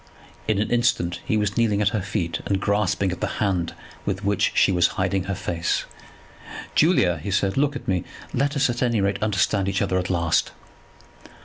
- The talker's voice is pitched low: Yes, low, 100 Hz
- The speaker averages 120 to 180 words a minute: No, average, 195 wpm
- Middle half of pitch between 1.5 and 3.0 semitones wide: Yes, average, 2.7 semitones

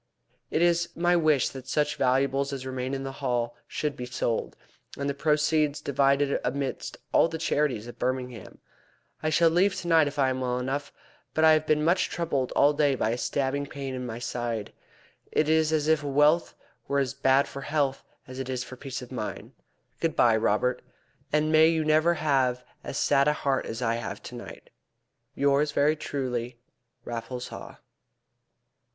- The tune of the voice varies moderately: Yes, average, 3.2 semitones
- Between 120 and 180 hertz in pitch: Yes, medium, 140 Hz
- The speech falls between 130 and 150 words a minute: No, average, 180 wpm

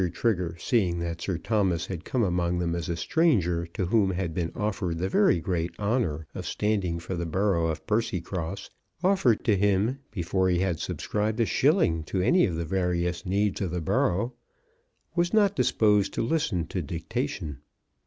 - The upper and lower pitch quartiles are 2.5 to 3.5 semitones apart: No, average, 4.0 semitones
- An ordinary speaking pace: Yes, average, 175 wpm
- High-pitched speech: No, very low, 95 Hz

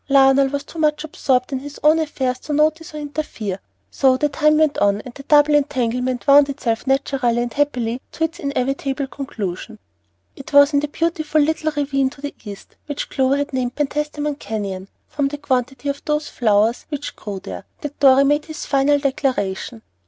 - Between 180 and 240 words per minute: Yes, average, 185 wpm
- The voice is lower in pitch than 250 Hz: No, very high, 275 Hz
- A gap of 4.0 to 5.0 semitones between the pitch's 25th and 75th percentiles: No, average, 2.8 semitones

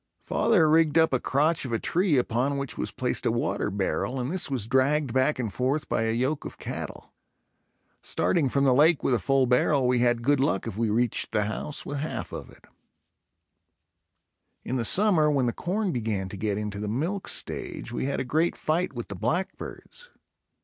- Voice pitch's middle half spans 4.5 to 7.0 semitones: Yes, average, 4.8 semitones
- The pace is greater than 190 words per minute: Yes, average, 200 wpm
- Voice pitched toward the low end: Yes, low, 130 Hz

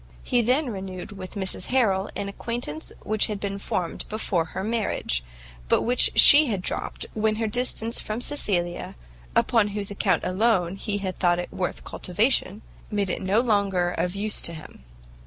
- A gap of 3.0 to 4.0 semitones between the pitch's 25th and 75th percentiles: Yes, average, 3.3 semitones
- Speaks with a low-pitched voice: No, high, 200 Hz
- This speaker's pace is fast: No, average, 170 wpm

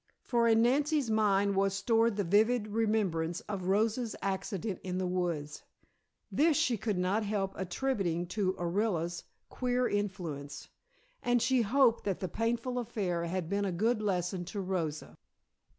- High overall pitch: Yes, high, 200 Hz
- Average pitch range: Yes, average, 4.1 semitones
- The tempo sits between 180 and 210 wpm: No, average, 150 wpm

